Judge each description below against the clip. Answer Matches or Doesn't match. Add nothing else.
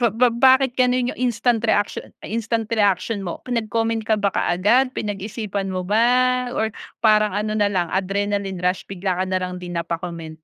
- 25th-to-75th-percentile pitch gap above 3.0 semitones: Matches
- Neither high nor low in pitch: Doesn't match